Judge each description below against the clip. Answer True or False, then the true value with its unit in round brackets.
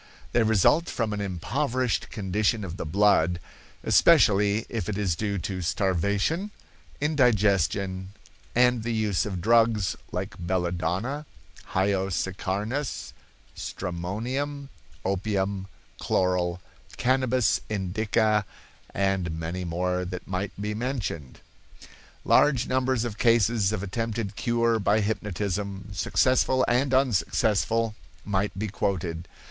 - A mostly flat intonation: False (3.8 semitones)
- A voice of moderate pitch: False (105 Hz)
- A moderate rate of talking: False (105 wpm)